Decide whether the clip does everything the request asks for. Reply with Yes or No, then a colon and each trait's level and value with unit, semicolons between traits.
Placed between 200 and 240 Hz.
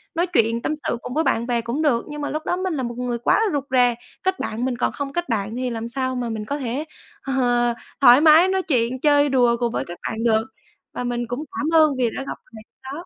No: very high, 255 Hz